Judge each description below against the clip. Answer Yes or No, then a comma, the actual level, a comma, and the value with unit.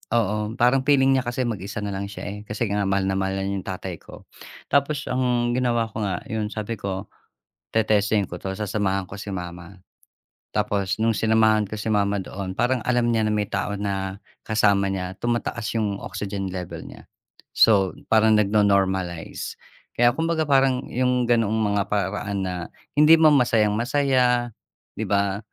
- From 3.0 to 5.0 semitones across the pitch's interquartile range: Yes, average, 3.6 semitones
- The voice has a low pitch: Yes, low, 105 Hz